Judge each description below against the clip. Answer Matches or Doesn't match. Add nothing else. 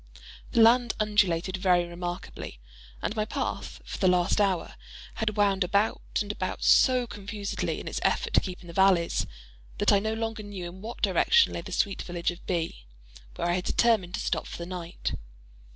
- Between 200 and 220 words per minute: Doesn't match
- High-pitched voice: Matches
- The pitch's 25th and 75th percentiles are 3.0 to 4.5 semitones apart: Matches